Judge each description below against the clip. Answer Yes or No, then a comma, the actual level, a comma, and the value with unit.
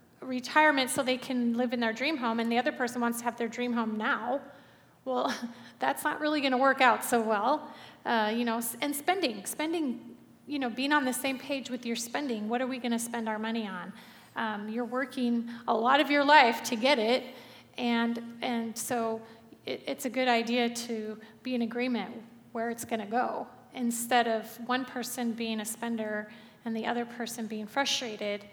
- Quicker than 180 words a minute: Yes, average, 200 wpm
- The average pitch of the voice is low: No, high, 240 Hz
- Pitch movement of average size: No, narrow, 2.0 semitones